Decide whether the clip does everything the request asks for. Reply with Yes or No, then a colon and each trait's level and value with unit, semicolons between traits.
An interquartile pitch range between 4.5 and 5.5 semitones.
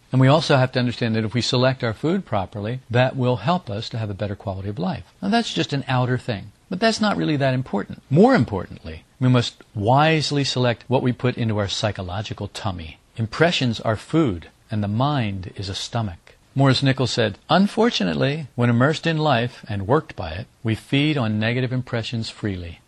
Yes: average, 4.9 semitones